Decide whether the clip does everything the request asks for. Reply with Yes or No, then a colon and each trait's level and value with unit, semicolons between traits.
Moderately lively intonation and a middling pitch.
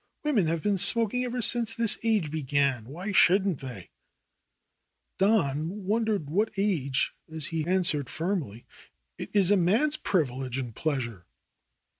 No: wide, 6.9 semitones; medium, 175 Hz